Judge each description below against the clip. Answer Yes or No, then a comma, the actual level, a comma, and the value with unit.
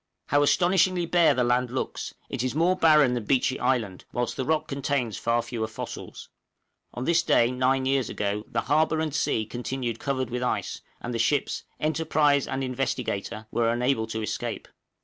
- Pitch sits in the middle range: No, low, 130 Hz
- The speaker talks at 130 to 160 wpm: No, average, 175 wpm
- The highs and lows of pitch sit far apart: No, average, 3.7 semitones